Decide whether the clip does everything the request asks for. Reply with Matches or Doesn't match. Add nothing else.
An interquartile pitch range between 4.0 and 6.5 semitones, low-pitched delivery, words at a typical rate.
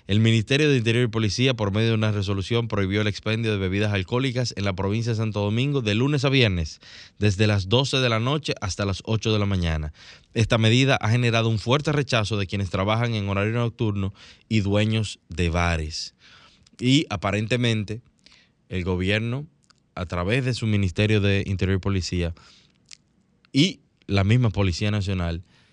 Doesn't match